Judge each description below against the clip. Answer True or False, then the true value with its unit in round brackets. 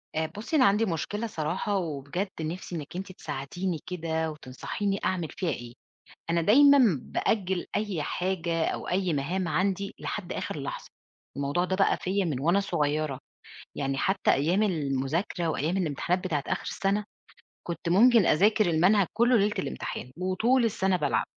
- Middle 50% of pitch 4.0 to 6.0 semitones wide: True (4.3 semitones)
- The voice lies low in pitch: False (180 Hz)